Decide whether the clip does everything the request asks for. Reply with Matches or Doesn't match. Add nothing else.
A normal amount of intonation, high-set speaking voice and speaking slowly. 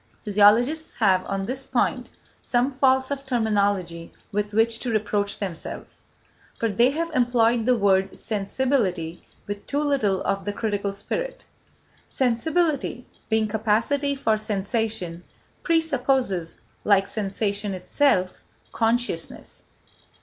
Matches